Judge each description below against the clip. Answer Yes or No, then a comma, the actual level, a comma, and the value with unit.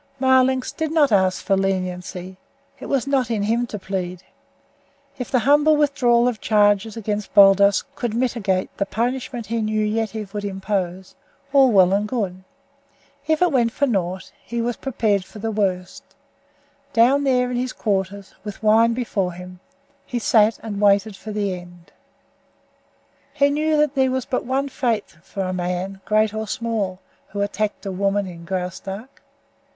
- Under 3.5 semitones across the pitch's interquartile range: No, average, 4.3 semitones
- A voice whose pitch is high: Yes, high, 215 Hz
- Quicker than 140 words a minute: Yes, average, 165 wpm